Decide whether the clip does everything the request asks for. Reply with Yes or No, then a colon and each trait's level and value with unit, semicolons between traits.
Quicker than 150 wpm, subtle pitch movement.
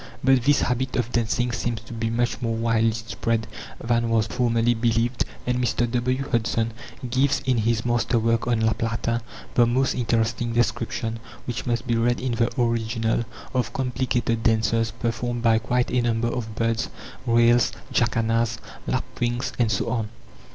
Yes: average, 160 wpm; narrow, 1.1 semitones